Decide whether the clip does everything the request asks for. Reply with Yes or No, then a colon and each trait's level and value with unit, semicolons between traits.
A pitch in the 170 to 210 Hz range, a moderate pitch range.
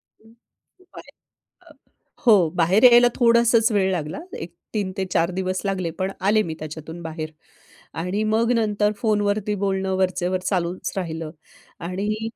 Yes: high, 190 Hz; average, 3.7 semitones